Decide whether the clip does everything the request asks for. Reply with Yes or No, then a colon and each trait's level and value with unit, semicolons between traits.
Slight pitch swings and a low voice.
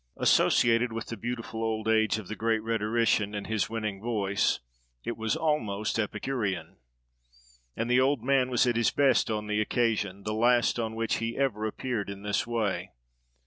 Yes: narrow, 2.1 semitones; low, 110 Hz